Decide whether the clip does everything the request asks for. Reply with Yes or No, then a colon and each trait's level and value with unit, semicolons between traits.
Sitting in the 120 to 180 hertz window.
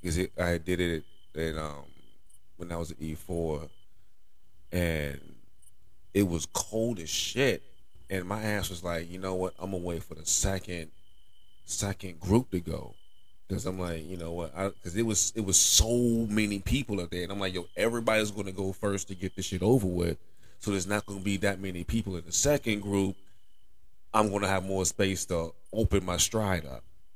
No: very low, 95 Hz